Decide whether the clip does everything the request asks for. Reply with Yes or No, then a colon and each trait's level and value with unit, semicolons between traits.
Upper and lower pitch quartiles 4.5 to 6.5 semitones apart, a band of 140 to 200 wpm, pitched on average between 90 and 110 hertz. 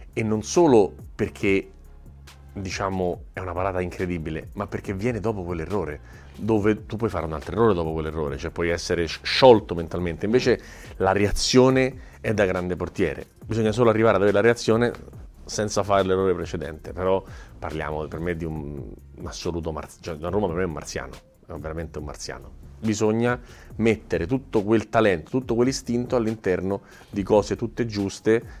Yes: average, 5.0 semitones; average, 165 wpm; very low, 95 Hz